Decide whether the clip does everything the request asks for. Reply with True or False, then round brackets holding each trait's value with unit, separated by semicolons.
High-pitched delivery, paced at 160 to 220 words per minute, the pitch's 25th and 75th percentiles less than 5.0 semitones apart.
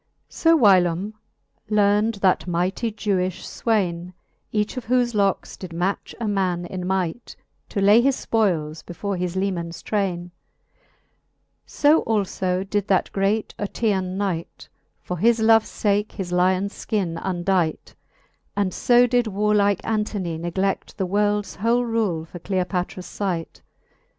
False (195 Hz; 135 wpm; 2.9 semitones)